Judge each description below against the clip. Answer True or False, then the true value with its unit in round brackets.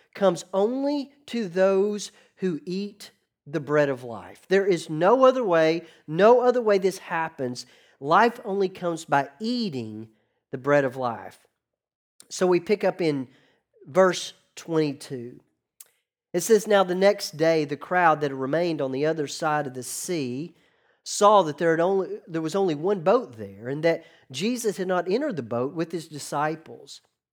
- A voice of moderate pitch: True (165 Hz)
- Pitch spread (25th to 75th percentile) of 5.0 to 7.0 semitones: True (5.5 semitones)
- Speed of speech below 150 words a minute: False (165 wpm)